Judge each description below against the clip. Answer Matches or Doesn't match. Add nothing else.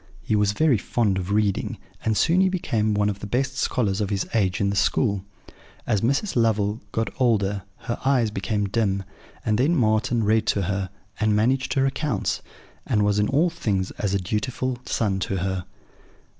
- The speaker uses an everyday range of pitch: Matches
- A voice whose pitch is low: Matches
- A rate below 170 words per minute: Doesn't match